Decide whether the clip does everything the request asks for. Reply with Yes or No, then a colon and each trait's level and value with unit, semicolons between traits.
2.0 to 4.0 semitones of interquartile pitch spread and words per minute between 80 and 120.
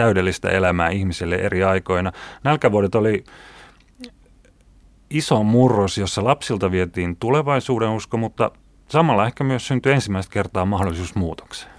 No: average, 5.1 semitones; average, 115 wpm